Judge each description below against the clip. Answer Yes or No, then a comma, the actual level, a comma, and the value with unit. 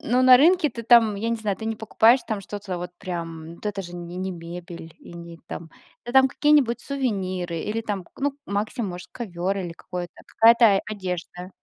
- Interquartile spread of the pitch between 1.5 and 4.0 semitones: No, average, 4.7 semitones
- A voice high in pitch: Yes, high, 200 Hz